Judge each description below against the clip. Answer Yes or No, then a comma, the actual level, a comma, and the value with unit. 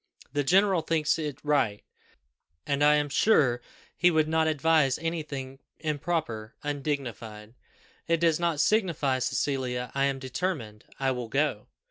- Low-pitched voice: No, medium, 145 Hz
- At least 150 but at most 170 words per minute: No, average, 140 wpm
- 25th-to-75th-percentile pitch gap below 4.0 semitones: Yes, average, 3.6 semitones